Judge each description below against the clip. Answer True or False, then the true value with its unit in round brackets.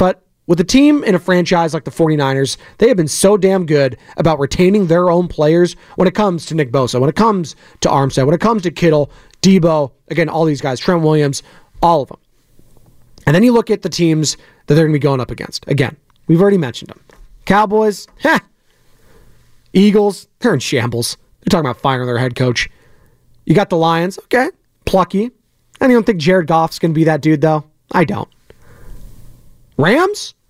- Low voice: False (165 Hz)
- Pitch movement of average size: True (4.6 semitones)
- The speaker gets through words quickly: False (195 wpm)